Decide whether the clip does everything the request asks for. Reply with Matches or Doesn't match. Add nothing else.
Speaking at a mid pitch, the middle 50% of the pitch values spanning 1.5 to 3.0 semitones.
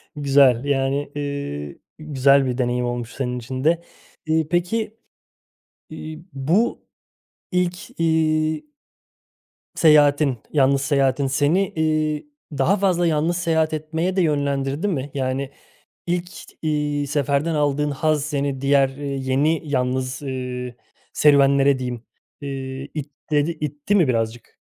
Matches